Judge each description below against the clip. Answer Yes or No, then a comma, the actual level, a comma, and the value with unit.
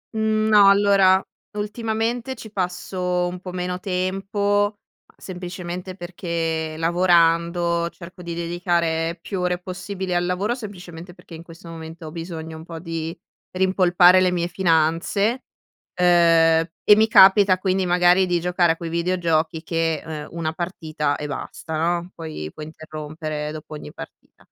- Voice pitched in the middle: Yes, medium, 175 Hz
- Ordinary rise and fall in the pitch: No, narrow, 2.3 semitones